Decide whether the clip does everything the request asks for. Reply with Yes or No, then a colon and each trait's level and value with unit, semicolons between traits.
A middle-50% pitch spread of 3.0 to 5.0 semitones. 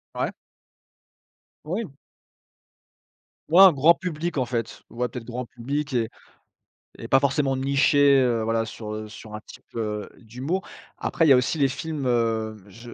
Yes: average, 4.1 semitones